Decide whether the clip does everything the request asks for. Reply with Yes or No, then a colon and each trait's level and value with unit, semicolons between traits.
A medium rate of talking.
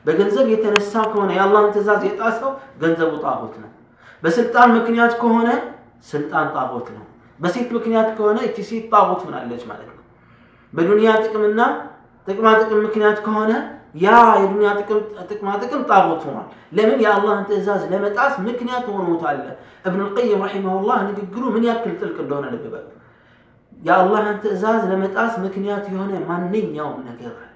No: fast, 145 wpm